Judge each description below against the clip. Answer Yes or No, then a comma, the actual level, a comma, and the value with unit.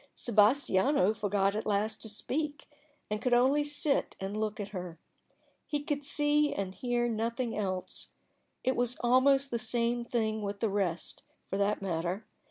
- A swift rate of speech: No, average, 160 wpm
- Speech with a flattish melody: No, average, 4.4 semitones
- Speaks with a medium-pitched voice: No, high, 225 Hz